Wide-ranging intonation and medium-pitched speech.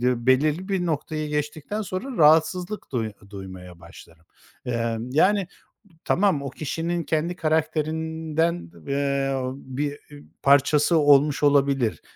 No: average, 3.6 semitones; medium, 150 Hz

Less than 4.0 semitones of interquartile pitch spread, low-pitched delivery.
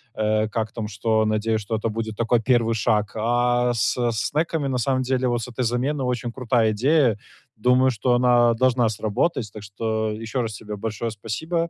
Yes: narrow, 2.5 semitones; low, 115 Hz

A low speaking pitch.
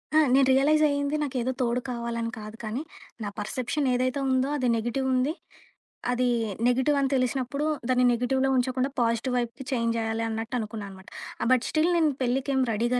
No: very high, 250 Hz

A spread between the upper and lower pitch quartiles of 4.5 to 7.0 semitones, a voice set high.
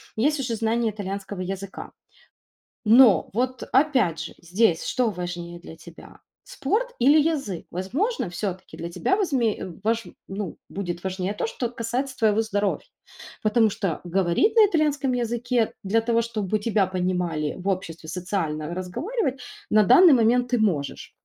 Yes: wide, 5.4 semitones; high, 215 Hz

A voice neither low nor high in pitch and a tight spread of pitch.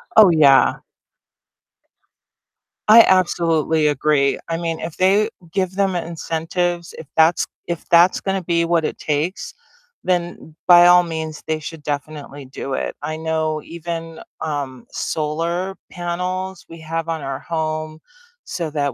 Yes: medium, 165 Hz; narrow, 2.2 semitones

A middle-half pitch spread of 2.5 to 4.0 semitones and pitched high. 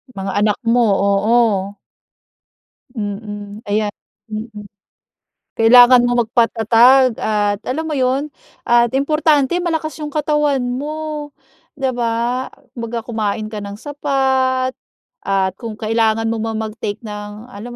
Yes: average, 3.7 semitones; high, 235 Hz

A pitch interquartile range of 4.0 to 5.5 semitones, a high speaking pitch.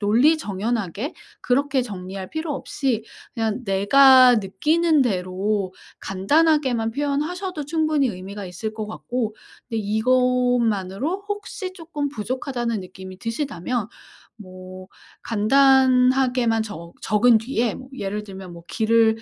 Yes: average, 5.2 semitones; high, 230 Hz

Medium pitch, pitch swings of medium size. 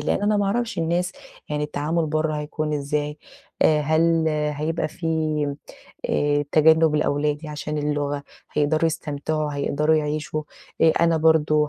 No: medium, 155 Hz; narrow, 1.4 semitones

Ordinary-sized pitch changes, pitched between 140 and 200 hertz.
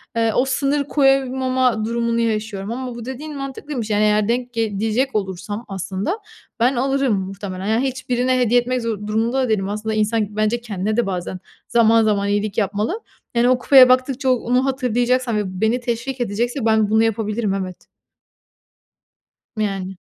No: average, 3.3 semitones; high, 230 Hz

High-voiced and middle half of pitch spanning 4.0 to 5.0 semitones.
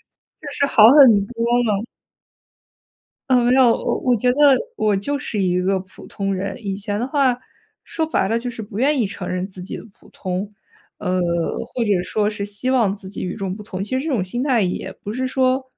Yes: high, 210 Hz; average, 4.7 semitones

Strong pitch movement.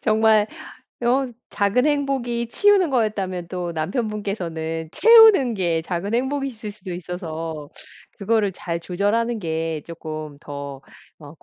Yes: wide, 6.2 semitones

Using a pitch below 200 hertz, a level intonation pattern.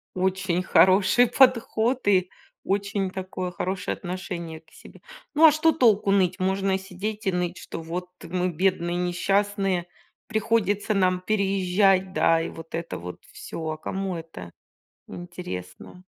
Yes: medium, 185 Hz; narrow, 2.2 semitones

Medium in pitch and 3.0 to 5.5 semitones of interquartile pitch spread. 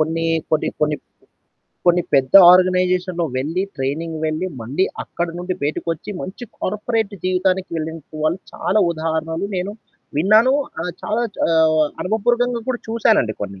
Yes: medium, 180 Hz; average, 3.8 semitones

